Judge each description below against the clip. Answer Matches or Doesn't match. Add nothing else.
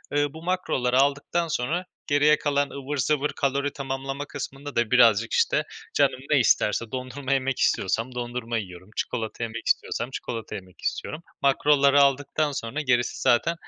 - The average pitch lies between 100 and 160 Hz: Matches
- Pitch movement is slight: Doesn't match